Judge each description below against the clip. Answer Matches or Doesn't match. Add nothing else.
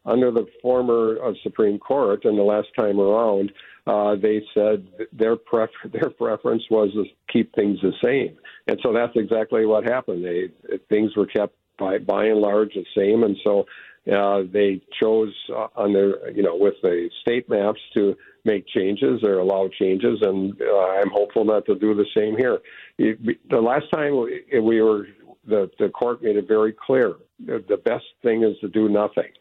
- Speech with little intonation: Matches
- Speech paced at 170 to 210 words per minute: Matches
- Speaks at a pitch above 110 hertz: Doesn't match